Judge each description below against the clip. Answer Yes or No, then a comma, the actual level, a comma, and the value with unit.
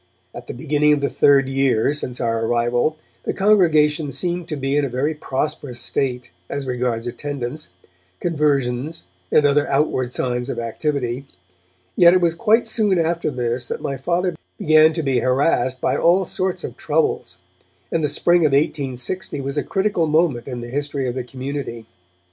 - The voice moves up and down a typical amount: Yes, average, 4.1 semitones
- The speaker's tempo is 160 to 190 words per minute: Yes, average, 170 wpm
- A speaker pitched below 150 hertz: Yes, medium, 140 Hz